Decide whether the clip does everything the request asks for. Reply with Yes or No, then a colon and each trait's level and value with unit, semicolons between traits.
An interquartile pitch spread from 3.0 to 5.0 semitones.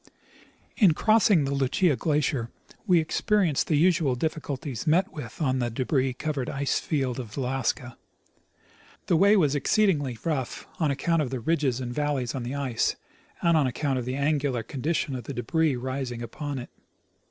Yes: average, 3.7 semitones